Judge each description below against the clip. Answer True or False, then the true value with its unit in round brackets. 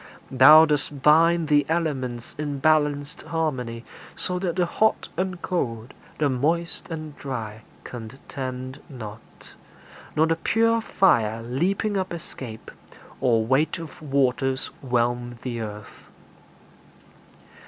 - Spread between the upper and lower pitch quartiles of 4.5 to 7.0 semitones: True (5.1 semitones)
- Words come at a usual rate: False (115 wpm)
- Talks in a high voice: False (140 Hz)